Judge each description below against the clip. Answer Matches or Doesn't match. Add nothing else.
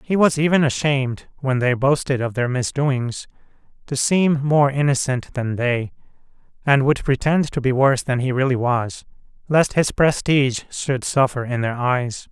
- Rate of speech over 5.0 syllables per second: Doesn't match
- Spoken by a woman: Doesn't match